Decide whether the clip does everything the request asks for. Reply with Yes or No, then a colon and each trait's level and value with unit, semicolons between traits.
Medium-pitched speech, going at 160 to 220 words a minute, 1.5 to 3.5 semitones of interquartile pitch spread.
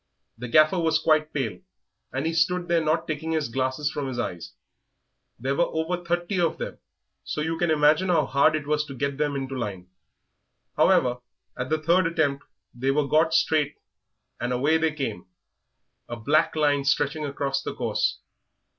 Yes: medium, 150 Hz; average, 180 wpm; average, 3.1 semitones